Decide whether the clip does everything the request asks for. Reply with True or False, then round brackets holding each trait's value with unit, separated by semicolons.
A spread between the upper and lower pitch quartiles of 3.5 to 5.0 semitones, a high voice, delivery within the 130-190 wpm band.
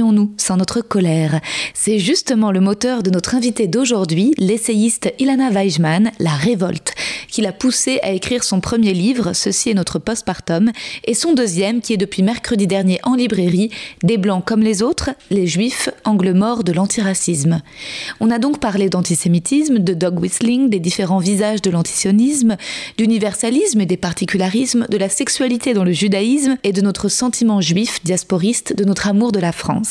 True (3.9 semitones; 210 Hz; 170 wpm)